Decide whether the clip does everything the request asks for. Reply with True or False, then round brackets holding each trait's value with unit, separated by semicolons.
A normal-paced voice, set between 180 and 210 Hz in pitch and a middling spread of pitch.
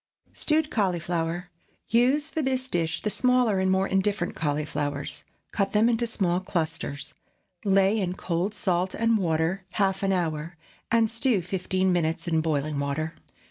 True (145 wpm; 185 Hz; 4.8 semitones)